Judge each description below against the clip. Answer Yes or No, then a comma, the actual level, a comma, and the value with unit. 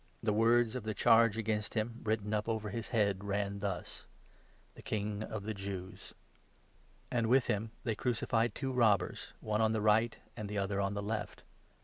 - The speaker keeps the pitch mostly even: Yes, narrow, 1.9 semitones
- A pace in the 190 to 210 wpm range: Yes, average, 200 wpm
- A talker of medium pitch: No, low, 110 Hz